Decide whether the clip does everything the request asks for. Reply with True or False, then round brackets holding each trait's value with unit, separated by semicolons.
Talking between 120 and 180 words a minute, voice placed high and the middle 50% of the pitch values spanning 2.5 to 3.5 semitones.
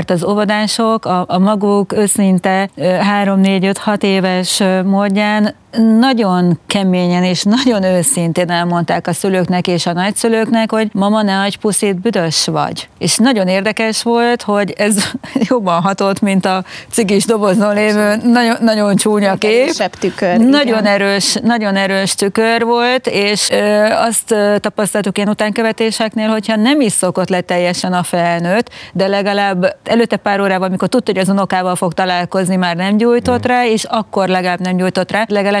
True (145 wpm; 205 Hz; 2.9 semitones)